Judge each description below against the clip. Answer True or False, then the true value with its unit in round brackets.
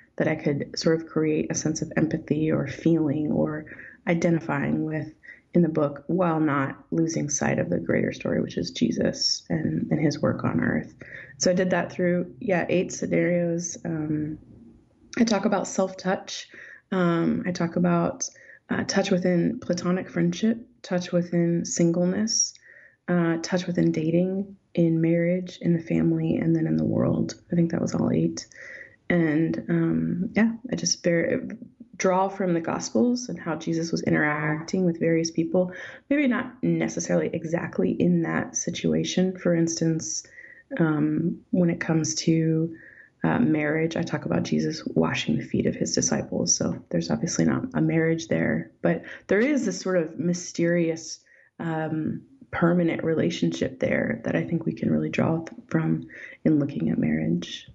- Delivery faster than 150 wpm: True (160 wpm)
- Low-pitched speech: False (170 Hz)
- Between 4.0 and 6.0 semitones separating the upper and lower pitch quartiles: False (2.9 semitones)